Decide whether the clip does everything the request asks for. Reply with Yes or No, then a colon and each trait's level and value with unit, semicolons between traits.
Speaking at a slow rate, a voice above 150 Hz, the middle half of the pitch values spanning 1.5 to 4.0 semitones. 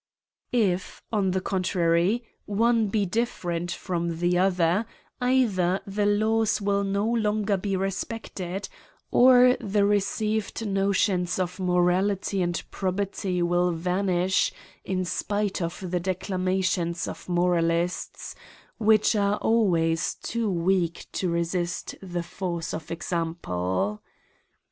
Yes: slow, 115 wpm; medium, 185 Hz; average, 2.8 semitones